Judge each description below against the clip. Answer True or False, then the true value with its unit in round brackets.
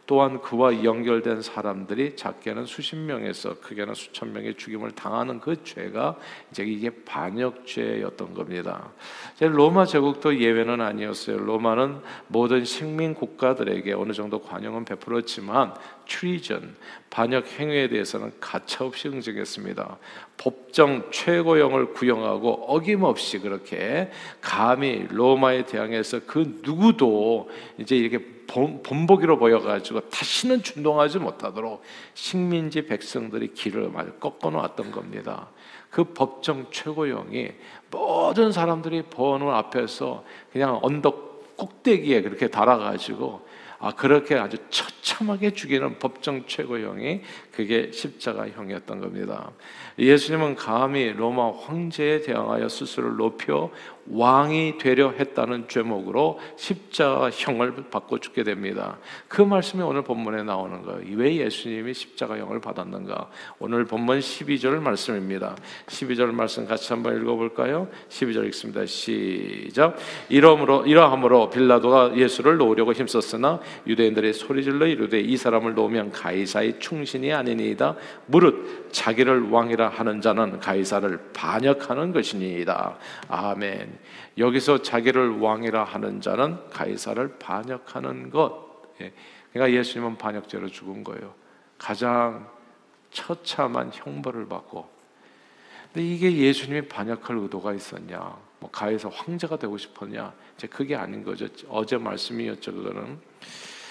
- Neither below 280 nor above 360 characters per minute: True (305 characters per minute)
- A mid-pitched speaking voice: False (125 Hz)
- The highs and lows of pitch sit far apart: False (4.5 semitones)